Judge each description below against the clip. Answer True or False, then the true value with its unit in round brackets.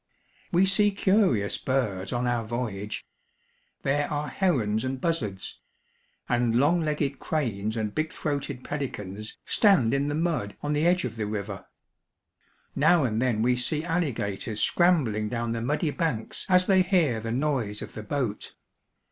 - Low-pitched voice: True (130 Hz)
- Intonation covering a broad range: True (6.2 semitones)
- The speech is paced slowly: False (155 wpm)